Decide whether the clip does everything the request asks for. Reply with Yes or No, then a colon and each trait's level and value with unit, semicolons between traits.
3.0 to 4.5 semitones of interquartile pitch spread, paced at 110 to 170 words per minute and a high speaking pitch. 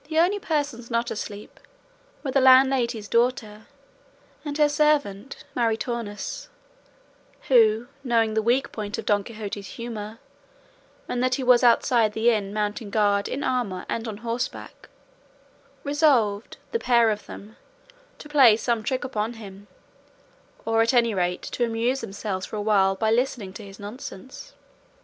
Yes: average, 3.4 semitones; average, 150 wpm; high, 230 Hz